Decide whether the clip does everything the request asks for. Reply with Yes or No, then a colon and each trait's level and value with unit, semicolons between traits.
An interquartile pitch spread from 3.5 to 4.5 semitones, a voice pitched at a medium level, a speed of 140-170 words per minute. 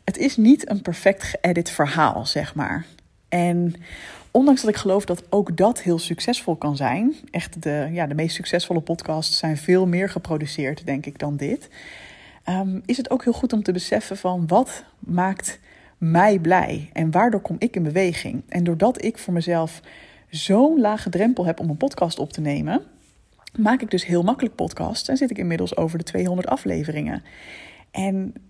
No: average, 4.2 semitones; medium, 180 Hz; average, 180 wpm